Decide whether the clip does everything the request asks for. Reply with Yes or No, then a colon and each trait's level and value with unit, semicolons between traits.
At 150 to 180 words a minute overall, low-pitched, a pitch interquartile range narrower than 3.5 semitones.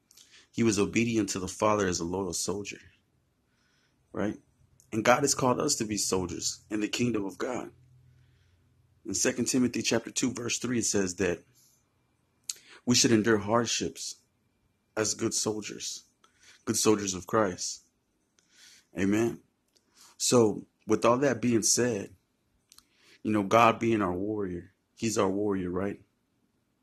No: average, 140 wpm; low, 110 Hz; average, 2.9 semitones